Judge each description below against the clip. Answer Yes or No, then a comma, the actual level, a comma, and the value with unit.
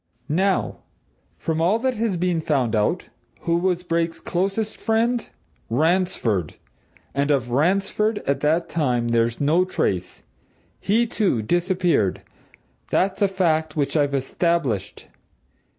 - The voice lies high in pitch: No, medium, 170 Hz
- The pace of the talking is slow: Yes, slow, 120 wpm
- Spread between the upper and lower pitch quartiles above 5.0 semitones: Yes, wide, 5.5 semitones